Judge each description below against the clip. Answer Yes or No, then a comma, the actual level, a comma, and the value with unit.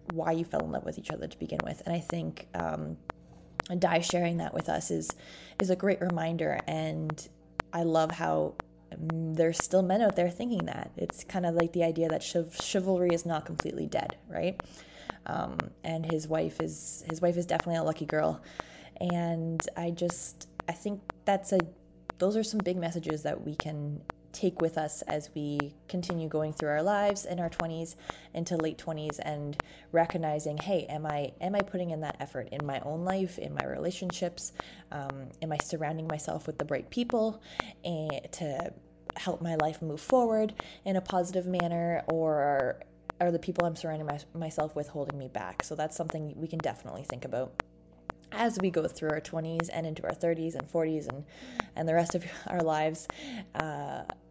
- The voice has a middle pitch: Yes, medium, 165 Hz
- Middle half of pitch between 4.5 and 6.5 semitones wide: No, average, 2.7 semitones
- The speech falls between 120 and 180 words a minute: No, average, 190 wpm